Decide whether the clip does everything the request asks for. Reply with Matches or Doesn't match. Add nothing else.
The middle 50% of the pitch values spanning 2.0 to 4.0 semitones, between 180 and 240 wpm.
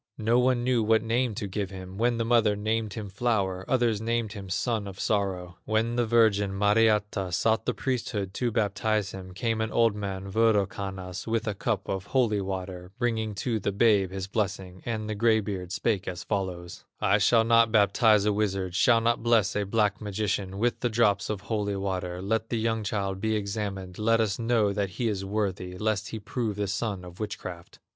Matches